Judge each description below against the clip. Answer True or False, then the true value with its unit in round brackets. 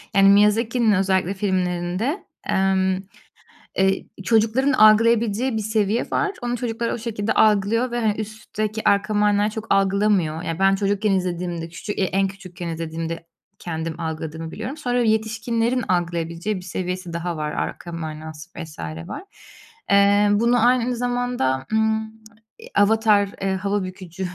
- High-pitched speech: True (200 Hz)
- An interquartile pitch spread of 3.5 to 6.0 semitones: True (3.8 semitones)